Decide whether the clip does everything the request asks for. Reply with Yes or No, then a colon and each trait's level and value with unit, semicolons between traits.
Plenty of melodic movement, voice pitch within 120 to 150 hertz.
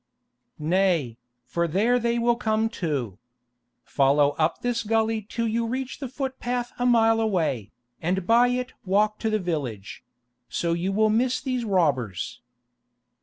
No: wide, 6.2 semitones; high, 215 Hz